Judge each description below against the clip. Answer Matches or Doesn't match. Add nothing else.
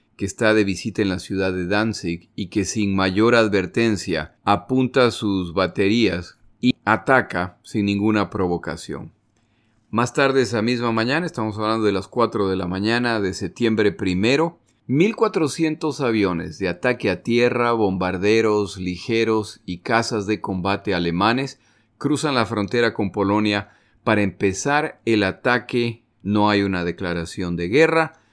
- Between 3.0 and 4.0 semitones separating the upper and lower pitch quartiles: Matches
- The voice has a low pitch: Matches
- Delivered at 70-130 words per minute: Doesn't match